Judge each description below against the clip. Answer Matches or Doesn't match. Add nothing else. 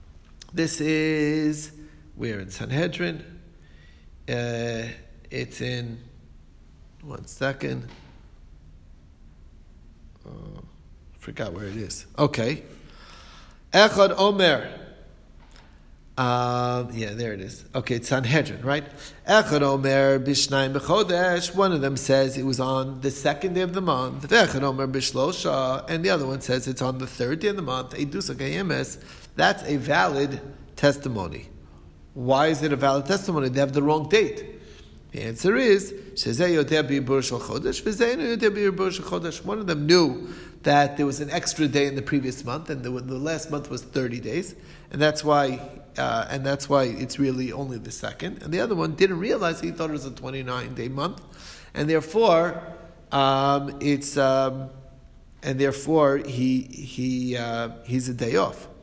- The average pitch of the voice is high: Doesn't match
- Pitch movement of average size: Matches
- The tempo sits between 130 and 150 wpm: Matches